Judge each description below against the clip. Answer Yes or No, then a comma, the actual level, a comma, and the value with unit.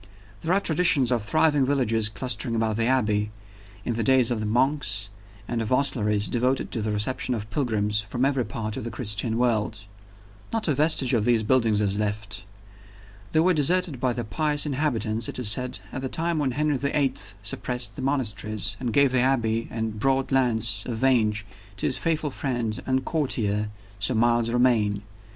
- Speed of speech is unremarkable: Yes, average, 185 wpm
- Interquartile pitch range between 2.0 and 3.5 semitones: No, average, 3.9 semitones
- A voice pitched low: Yes, low, 120 Hz